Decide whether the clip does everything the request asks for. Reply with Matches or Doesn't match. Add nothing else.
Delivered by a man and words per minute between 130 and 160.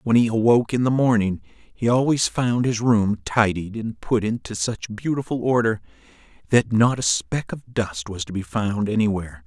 Doesn't match